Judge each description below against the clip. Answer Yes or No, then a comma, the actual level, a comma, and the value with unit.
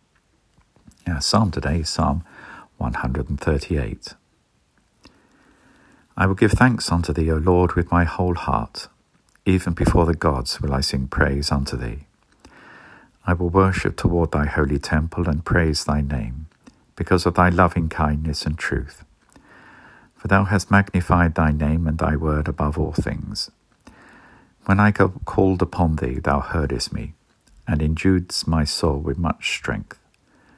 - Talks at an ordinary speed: Yes, average, 150 wpm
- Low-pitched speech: Yes, very low, 80 Hz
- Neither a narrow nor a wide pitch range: Yes, average, 3.2 semitones